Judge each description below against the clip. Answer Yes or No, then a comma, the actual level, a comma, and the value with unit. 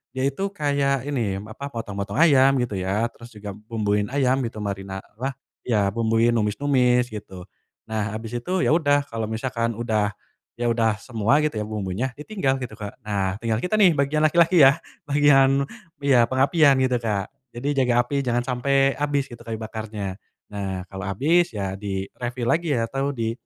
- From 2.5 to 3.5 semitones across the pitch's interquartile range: No, average, 4.6 semitones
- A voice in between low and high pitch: No, low, 120 Hz